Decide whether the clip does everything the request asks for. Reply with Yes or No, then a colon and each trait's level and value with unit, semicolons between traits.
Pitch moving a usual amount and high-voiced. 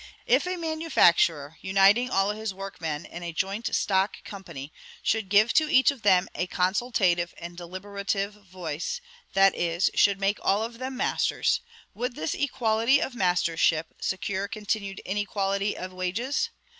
Yes: average, 3.6 semitones; high, 195 Hz